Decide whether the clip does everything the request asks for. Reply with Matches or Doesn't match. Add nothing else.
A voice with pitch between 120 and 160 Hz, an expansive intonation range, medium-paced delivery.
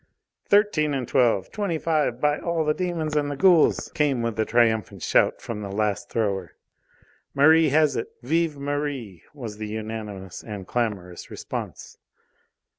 Matches